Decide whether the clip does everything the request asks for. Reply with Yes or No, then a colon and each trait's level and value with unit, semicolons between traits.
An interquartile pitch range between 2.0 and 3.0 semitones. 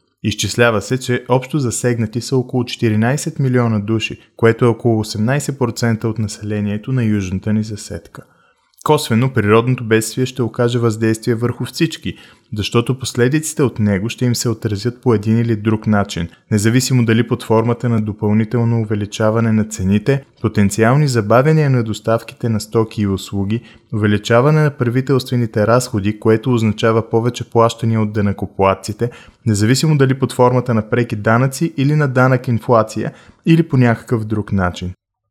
Yes: narrow, 2.4 semitones